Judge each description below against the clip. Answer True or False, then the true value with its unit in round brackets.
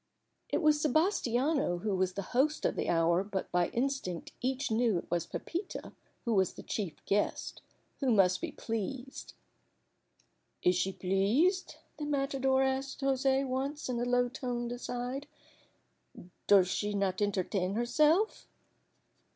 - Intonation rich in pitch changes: True (5.9 semitones)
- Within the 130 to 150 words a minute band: True (140 wpm)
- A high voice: True (245 Hz)